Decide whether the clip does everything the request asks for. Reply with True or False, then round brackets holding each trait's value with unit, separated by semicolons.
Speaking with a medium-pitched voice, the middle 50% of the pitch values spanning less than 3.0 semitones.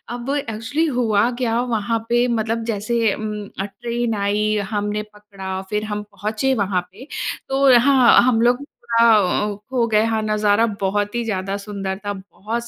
False (215 Hz; 2.4 semitones)